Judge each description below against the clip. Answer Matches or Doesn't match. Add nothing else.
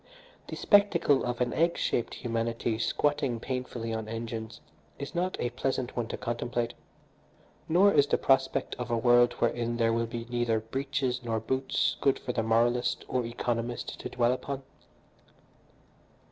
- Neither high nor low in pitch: Doesn't match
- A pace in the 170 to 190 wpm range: Doesn't match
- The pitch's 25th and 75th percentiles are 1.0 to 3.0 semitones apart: Matches